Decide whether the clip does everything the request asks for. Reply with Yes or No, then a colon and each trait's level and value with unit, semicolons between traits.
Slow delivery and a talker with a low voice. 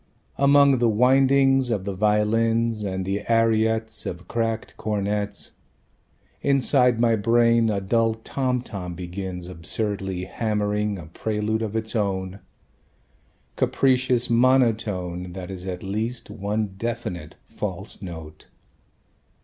Yes: slow, 115 wpm; low, 110 Hz